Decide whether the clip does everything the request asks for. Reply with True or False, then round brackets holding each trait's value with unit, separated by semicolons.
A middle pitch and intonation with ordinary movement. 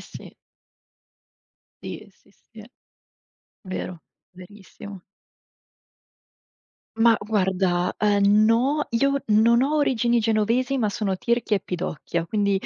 False (215 Hz; 3.4 semitones)